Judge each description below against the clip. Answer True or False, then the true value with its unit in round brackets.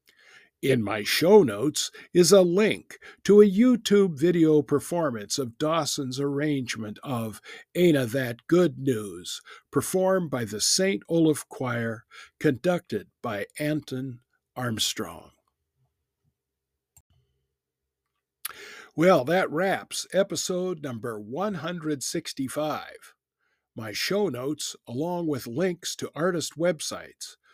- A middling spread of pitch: False (6.8 semitones)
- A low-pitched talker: False (150 Hz)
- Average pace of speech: False (100 wpm)